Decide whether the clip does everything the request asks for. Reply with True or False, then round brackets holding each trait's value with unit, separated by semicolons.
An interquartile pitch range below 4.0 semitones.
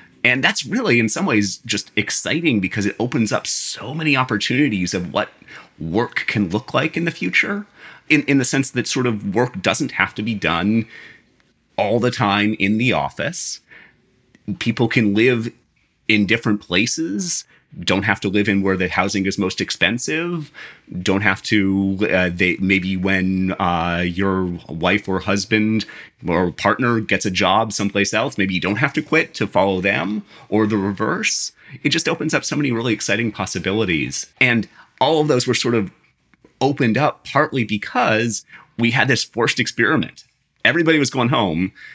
False (4.8 semitones)